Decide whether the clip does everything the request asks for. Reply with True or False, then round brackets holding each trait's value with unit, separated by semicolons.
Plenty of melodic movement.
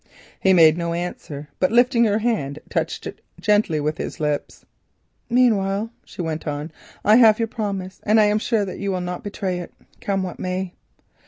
False (4.0 semitones)